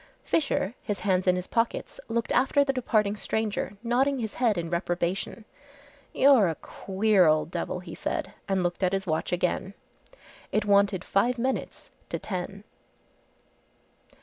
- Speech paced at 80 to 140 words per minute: No, average, 150 wpm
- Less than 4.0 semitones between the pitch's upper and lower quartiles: No, average, 4.3 semitones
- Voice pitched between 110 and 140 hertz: No, high, 200 Hz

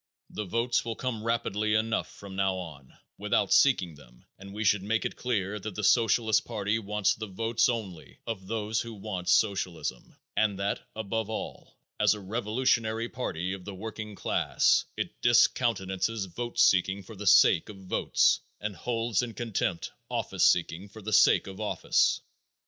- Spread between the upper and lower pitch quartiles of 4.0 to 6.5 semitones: No, average, 2.9 semitones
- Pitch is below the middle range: Yes, low, 105 Hz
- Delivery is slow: No, average, 165 wpm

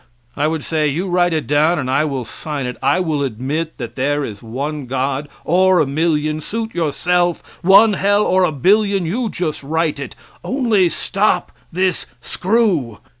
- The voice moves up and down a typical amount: Yes, average, 4.6 semitones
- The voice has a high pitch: No, medium, 160 Hz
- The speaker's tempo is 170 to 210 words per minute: Yes, average, 175 wpm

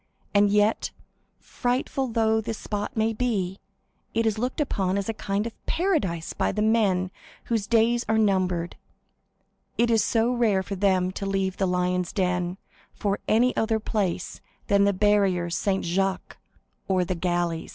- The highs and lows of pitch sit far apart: No, average, 3.2 semitones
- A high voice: Yes, high, 200 Hz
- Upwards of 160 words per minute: No, average, 155 wpm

